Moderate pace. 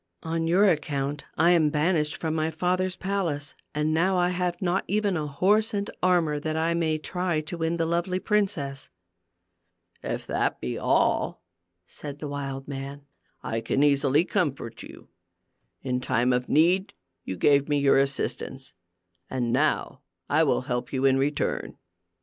Yes: average, 160 wpm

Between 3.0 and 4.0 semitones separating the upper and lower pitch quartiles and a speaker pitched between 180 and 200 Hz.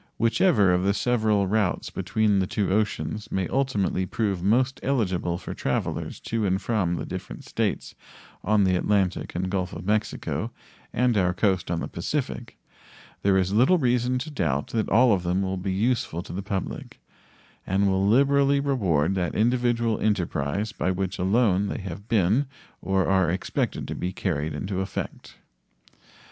No: average, 3.7 semitones; low, 100 Hz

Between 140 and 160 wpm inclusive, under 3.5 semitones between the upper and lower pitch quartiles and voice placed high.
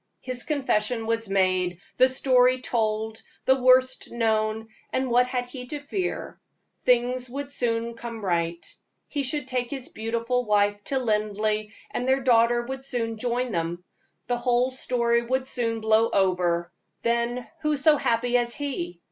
Yes: average, 155 wpm; average, 2.8 semitones; high, 240 Hz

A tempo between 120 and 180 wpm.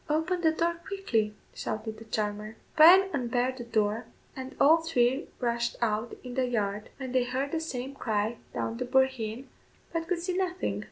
Yes: average, 175 wpm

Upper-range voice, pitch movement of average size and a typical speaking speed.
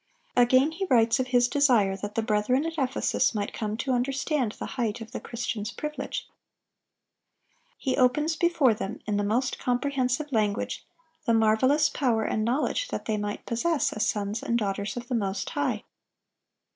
Yes: high, 240 Hz; average, 4.0 semitones; average, 170 wpm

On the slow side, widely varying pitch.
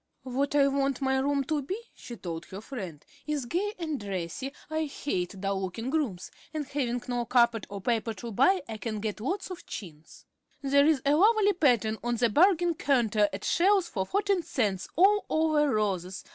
No: average, 185 wpm; wide, 6.7 semitones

